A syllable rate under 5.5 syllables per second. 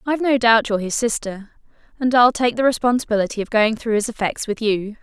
No: 6.0 syllables/s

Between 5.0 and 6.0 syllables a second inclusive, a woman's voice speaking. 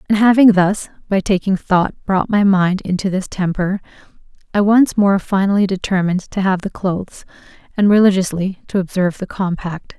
Yes: 5.2 syllables/s; female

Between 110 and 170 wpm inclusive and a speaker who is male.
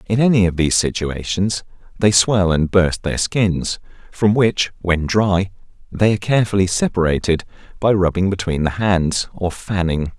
Yes: average, 155 wpm; male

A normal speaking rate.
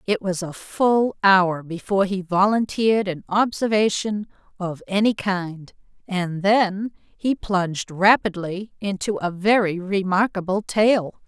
No: slow, 120 wpm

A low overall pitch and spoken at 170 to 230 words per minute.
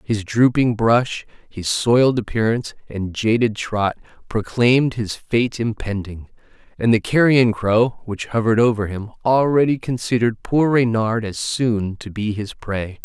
No: low, 115 Hz; average, 145 wpm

